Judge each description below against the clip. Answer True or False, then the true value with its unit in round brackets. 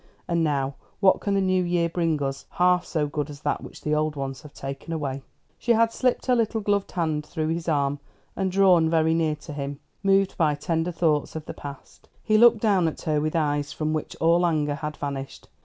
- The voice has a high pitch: False (160 Hz)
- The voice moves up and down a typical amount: True (3.6 semitones)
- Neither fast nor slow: False (220 wpm)